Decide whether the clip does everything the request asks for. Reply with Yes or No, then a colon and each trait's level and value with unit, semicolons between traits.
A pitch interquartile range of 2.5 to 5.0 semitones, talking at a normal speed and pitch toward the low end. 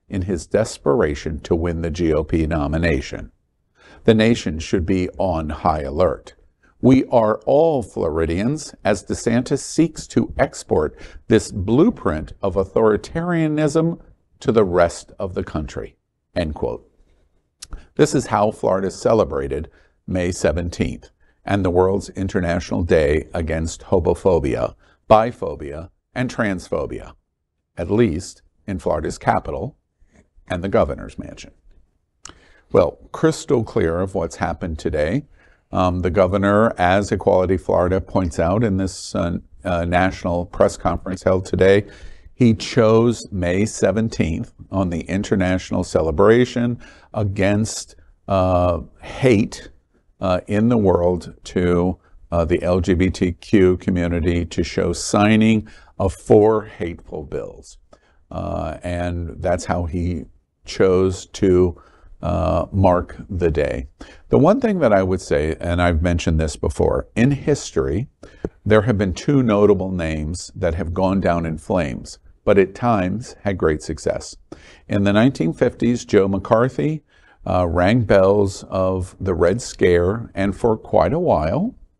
No: average, 3.3 semitones; slow, 125 wpm; very low, 90 Hz